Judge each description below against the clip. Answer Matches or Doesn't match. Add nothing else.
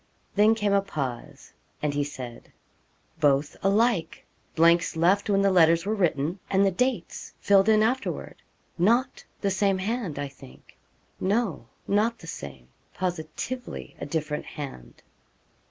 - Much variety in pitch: Matches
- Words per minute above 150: Doesn't match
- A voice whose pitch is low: Doesn't match